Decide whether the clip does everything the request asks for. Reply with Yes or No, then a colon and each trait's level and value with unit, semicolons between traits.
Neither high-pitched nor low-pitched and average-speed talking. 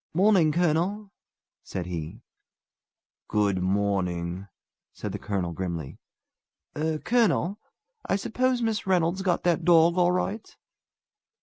No: medium, 165 Hz; slow, 115 wpm